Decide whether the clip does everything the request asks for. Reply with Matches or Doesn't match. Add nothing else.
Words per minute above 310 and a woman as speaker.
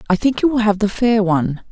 Doesn't match